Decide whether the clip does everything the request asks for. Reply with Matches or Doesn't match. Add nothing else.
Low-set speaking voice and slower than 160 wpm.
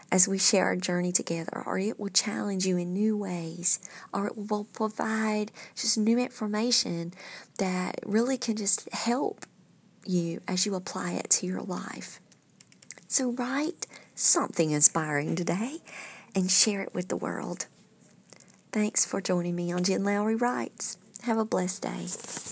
Doesn't match